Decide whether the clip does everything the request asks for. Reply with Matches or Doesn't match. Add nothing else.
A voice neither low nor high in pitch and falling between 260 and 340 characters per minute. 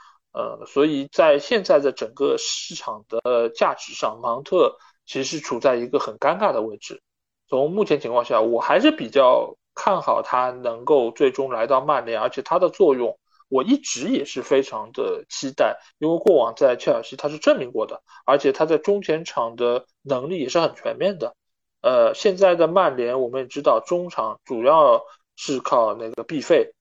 Matches